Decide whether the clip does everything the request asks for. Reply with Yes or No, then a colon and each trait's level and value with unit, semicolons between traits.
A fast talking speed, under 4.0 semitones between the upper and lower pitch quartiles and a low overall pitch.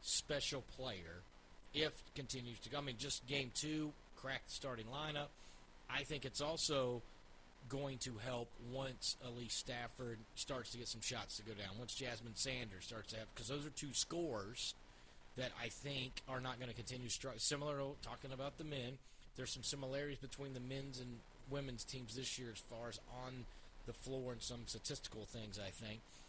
No: average, 185 wpm; average, 3.3 semitones; low, 125 Hz